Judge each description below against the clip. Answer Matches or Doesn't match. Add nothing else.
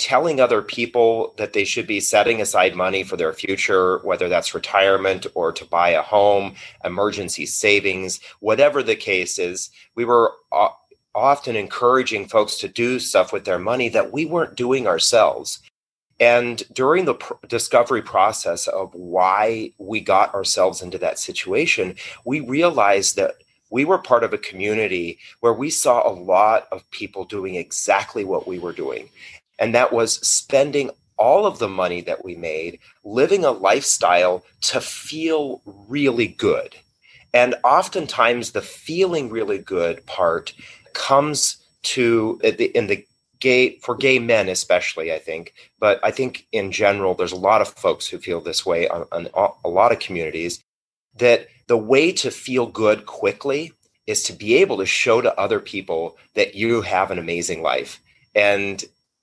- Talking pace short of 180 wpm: Matches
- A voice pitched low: Matches